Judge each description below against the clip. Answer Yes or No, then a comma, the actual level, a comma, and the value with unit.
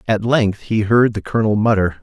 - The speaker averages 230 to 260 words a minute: No, fast, 205 wpm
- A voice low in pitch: Yes, low, 105 Hz